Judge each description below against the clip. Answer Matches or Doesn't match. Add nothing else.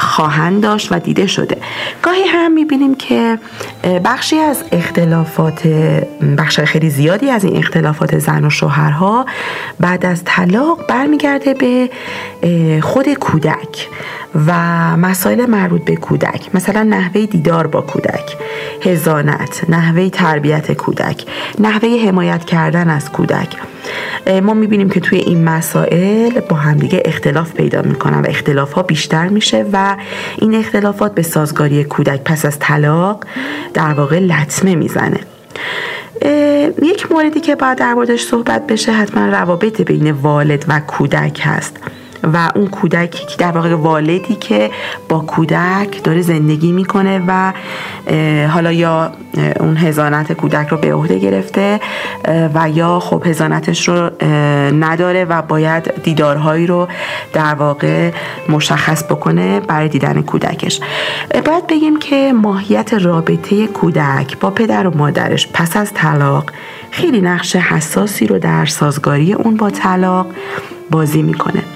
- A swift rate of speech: Doesn't match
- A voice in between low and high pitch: Matches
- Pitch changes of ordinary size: Matches